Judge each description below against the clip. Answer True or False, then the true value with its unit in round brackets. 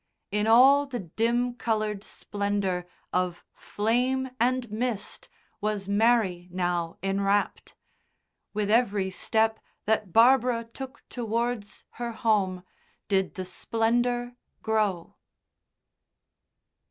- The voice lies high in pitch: True (220 Hz)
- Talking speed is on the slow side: True (95 wpm)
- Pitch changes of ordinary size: True (3.5 semitones)